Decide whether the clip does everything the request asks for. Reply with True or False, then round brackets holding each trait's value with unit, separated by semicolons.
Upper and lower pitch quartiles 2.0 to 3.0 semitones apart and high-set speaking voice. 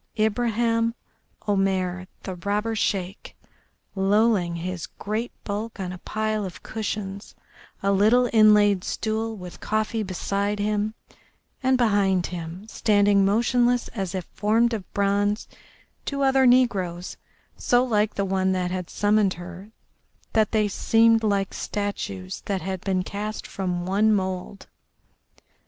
True (2.6 semitones; 205 Hz)